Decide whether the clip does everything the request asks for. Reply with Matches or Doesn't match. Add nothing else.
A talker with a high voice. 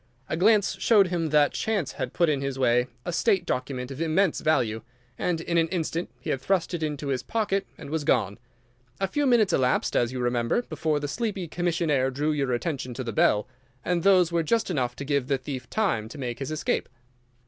Doesn't match